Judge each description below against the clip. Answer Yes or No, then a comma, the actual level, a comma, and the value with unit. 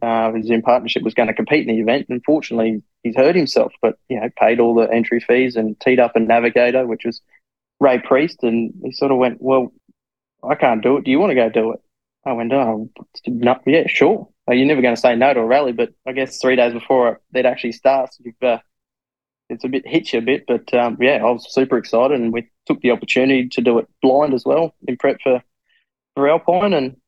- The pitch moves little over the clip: Yes, narrow, 2.1 semitones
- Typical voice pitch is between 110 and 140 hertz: Yes, low, 125 Hz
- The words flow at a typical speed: No, fast, 240 wpm